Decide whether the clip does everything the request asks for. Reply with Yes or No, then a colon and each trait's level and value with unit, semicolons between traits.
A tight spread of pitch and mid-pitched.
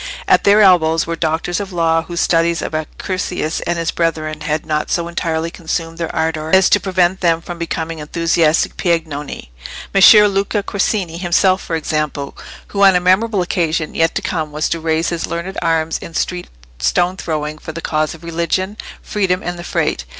Yes: narrow, 2.2 semitones; medium, 170 Hz